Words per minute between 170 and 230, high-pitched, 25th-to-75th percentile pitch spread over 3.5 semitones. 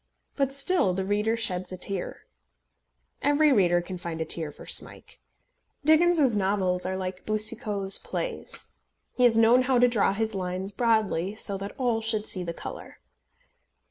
No: average, 160 wpm; high, 210 Hz; average, 4.6 semitones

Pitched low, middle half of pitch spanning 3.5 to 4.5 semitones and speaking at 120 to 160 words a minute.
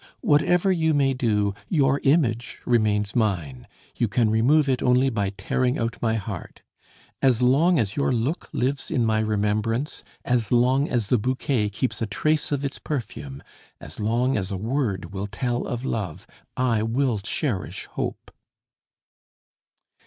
Yes: low, 120 Hz; average, 4.1 semitones; average, 155 wpm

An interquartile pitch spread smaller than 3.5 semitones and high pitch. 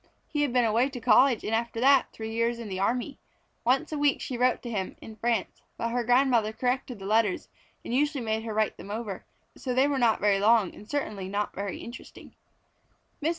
Yes: average, 2.9 semitones; high, 235 Hz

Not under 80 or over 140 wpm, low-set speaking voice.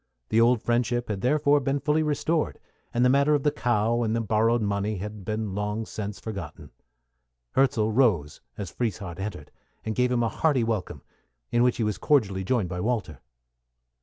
No: average, 180 wpm; low, 115 Hz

